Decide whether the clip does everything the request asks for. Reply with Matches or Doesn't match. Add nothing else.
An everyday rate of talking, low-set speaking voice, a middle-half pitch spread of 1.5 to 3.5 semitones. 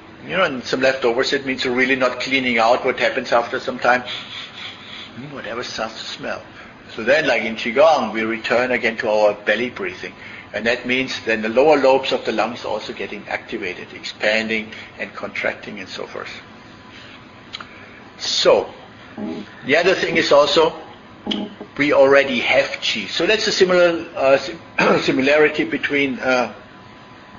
Matches